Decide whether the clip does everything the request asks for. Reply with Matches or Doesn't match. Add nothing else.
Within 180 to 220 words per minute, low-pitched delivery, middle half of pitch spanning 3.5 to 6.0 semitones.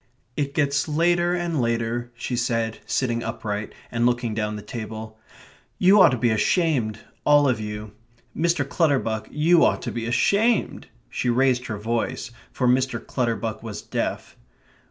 Doesn't match